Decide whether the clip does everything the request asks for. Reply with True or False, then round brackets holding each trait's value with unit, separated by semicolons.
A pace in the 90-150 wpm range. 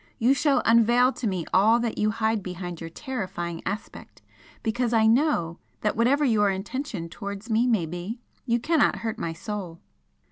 False (170 wpm)